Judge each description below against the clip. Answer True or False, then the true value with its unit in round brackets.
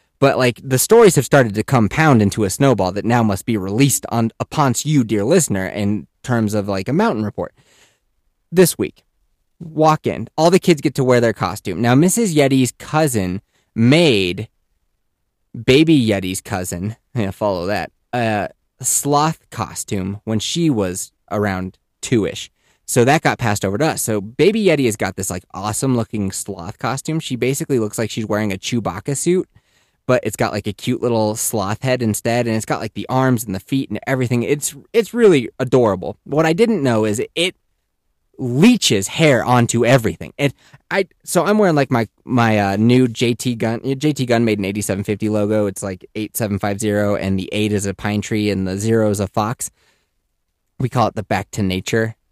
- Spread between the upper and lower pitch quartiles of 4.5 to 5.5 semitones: True (4.8 semitones)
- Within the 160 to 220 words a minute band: True (185 wpm)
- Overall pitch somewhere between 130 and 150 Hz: False (115 Hz)